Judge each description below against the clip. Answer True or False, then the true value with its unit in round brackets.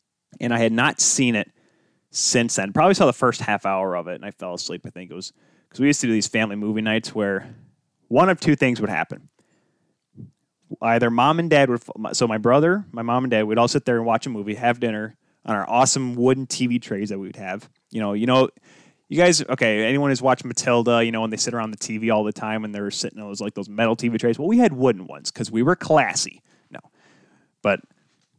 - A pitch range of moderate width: True (3.1 semitones)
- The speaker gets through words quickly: True (245 wpm)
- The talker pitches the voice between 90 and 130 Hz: True (115 Hz)